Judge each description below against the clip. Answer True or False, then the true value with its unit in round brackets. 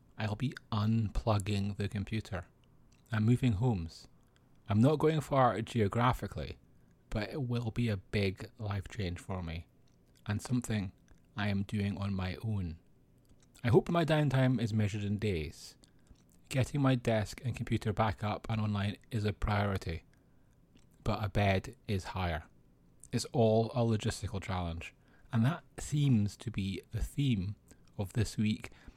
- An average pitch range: True (3.3 semitones)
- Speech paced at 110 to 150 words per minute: True (145 wpm)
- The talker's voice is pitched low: True (110 Hz)